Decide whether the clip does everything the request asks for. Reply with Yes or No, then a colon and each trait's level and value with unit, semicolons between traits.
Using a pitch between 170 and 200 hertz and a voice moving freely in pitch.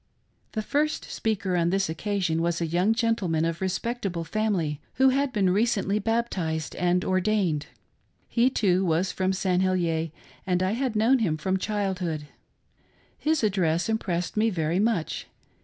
No: high, 190 Hz; average, 4.3 semitones